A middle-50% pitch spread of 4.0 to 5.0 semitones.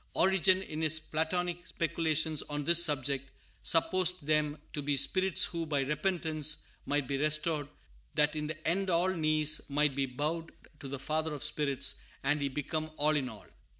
No: narrow, 2.4 semitones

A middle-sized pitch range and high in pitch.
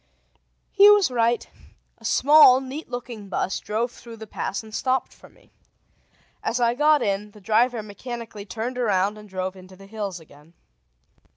Yes: average, 4.0 semitones; high, 225 Hz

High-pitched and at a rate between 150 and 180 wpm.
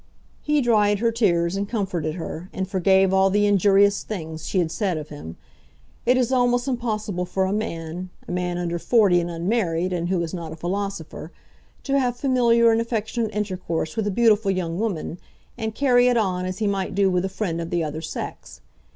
No: high, 195 Hz; average, 200 wpm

